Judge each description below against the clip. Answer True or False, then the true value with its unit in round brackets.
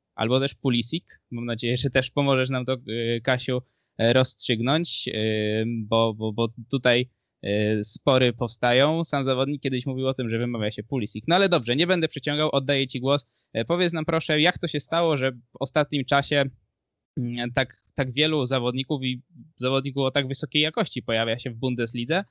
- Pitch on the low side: True (130 Hz)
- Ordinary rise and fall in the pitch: True (3.4 semitones)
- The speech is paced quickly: True (165 wpm)